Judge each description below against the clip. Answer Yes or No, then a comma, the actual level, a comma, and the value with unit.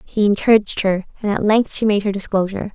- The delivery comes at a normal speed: No, fast, 220 wpm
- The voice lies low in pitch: No, high, 205 Hz